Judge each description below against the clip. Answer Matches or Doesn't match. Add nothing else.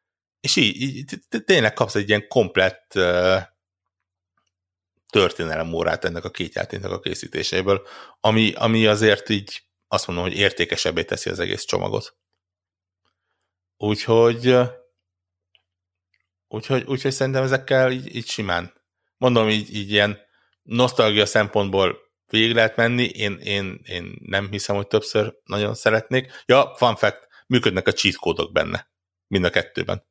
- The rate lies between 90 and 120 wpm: Doesn't match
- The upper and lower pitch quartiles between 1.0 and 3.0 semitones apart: Doesn't match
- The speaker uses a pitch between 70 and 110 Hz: Matches